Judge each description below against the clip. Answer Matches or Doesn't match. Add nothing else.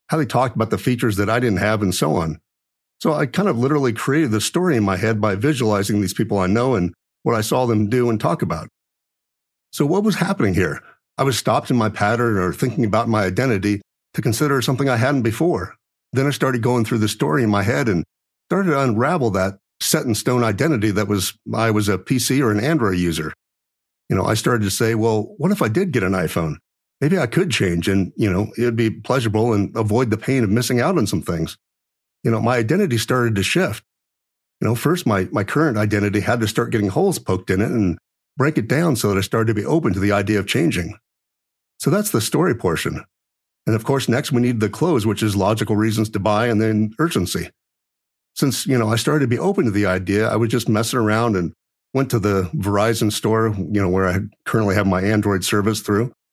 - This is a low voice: Matches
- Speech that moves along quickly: Matches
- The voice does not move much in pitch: Doesn't match